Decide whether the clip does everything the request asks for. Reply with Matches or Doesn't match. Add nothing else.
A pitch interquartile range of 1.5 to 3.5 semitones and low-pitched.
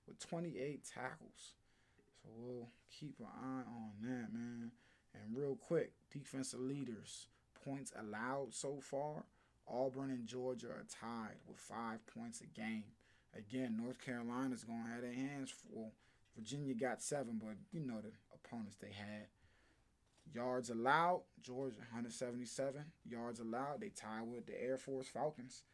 Matches